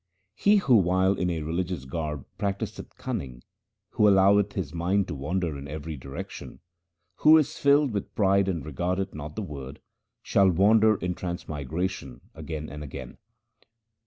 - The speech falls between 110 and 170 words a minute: Yes, average, 150 wpm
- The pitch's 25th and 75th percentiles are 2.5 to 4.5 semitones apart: No, average, 4.9 semitones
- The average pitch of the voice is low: Yes, very low, 90 Hz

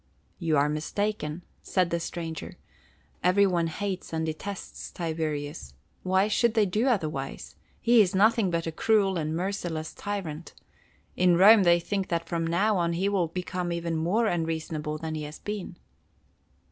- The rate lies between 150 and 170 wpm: Yes, average, 160 wpm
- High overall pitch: No, medium, 175 Hz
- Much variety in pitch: No, average, 3.7 semitones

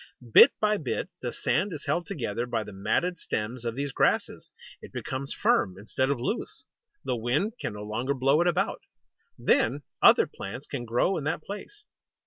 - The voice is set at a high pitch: No, low, 135 Hz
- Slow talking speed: No, average, 180 wpm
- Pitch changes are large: Yes, wide, 5.8 semitones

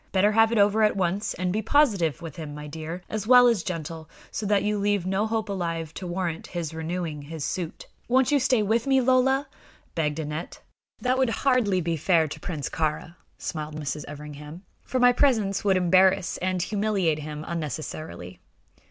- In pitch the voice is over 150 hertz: Yes, medium, 185 Hz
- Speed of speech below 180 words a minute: No, average, 185 wpm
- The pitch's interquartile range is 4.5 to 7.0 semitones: Yes, average, 5.2 semitones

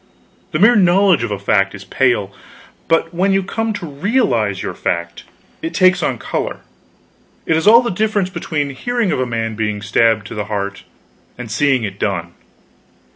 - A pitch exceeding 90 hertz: Yes, low, 135 Hz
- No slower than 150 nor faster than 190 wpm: Yes, average, 180 wpm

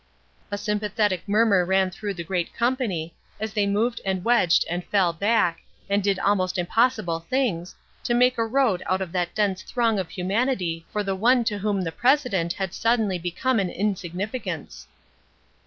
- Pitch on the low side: No, high, 200 Hz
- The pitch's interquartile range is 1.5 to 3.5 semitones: No, average, 4.0 semitones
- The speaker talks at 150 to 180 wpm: Yes, average, 170 wpm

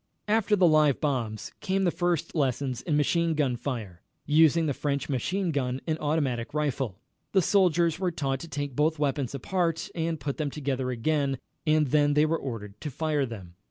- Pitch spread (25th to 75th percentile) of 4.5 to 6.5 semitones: No, average, 3.6 semitones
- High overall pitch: No, medium, 145 Hz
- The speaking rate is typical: Yes, average, 185 wpm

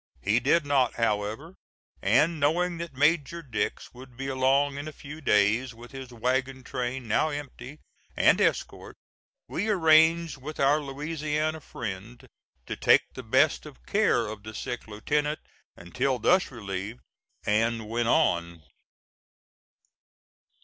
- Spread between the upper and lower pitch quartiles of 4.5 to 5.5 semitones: Yes, average, 4.8 semitones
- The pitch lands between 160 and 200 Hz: No, low, 130 Hz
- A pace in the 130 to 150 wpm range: Yes, slow, 135 wpm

